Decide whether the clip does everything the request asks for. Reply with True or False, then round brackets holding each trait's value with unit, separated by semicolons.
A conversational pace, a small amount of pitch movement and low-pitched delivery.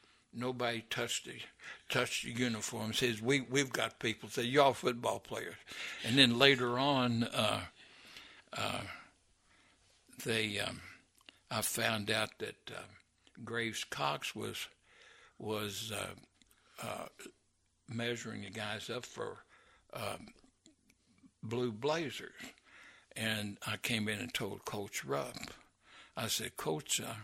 False (120 wpm; 2.2 semitones; 115 Hz)